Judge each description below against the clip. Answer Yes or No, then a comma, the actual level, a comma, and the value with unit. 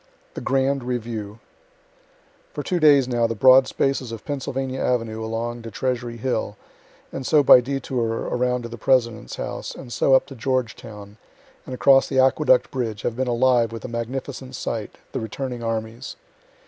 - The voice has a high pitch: No, low, 125 Hz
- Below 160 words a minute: No, average, 165 wpm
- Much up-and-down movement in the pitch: No, narrow, 2.5 semitones